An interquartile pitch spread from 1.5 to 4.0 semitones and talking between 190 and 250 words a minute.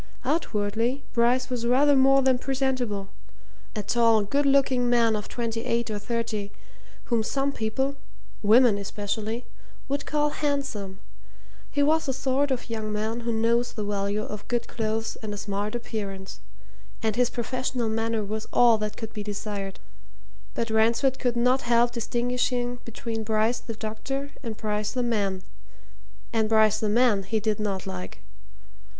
No: average, 2.8 semitones; average, 155 wpm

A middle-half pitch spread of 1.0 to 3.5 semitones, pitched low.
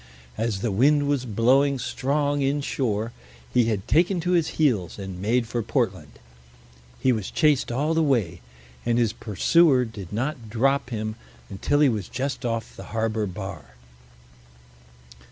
No: average, 4.8 semitones; low, 120 Hz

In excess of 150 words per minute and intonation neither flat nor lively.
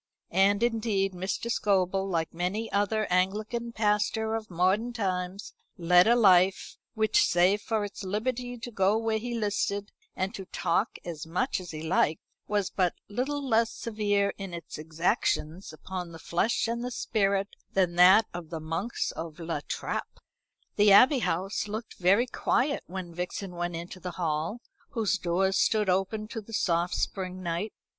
Yes: average, 165 wpm; average, 3.6 semitones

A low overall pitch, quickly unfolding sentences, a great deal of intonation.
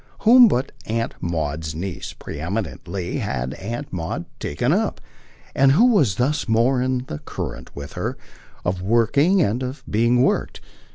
No: low, 115 Hz; average, 155 wpm; wide, 7.4 semitones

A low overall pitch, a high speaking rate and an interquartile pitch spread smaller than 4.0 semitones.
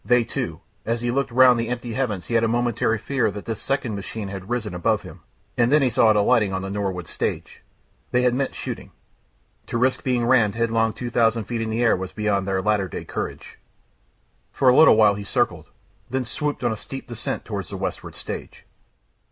Yes: low, 115 Hz; fast, 215 wpm; average, 3.1 semitones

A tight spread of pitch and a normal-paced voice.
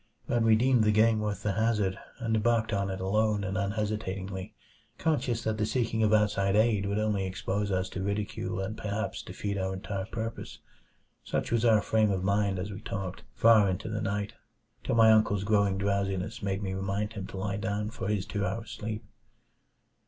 Yes: narrow, 2.1 semitones; average, 190 wpm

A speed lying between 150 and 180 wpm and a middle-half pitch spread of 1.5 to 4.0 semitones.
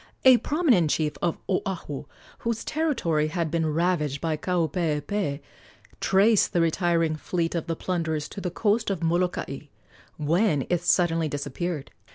No: average, 140 wpm; average, 3.1 semitones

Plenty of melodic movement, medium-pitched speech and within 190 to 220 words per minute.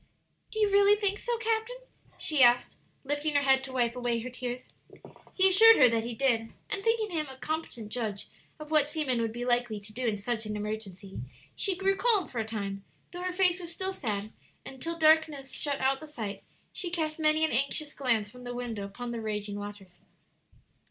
No: wide, 6.7 semitones; very high, 265 Hz; fast, 205 wpm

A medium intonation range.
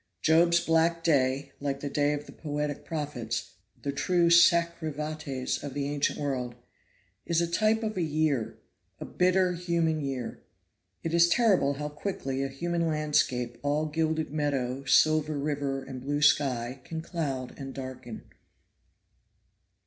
Yes: average, 3.4 semitones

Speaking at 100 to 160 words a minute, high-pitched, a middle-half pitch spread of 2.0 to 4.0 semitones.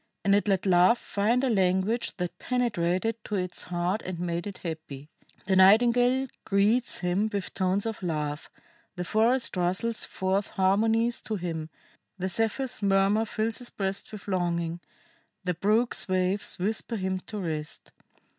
Yes: average, 150 wpm; high, 195 Hz; average, 3.7 semitones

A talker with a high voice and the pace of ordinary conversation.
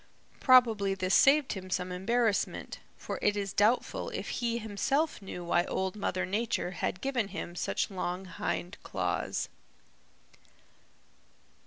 No: high, 200 Hz; slow, 130 wpm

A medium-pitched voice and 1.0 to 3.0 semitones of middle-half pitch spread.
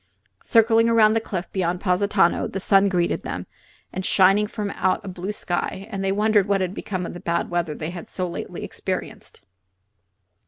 No: high, 195 Hz; narrow, 2.6 semitones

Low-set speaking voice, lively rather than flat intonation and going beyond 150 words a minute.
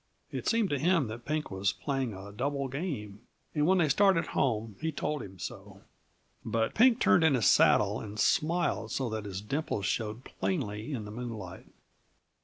Yes: low, 125 Hz; wide, 6.5 semitones; average, 180 wpm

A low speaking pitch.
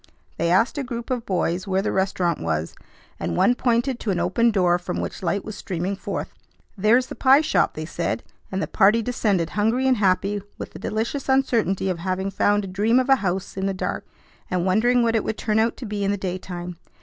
No: high, 200 Hz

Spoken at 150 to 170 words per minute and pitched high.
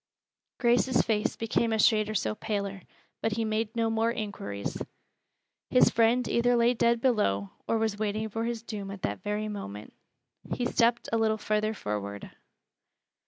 Yes: average, 165 wpm; high, 220 Hz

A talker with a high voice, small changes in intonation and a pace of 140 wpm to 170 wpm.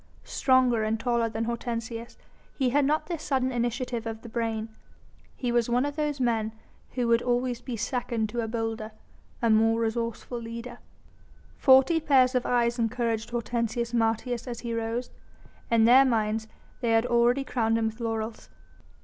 Yes: high, 235 Hz; narrow, 1.7 semitones; average, 165 wpm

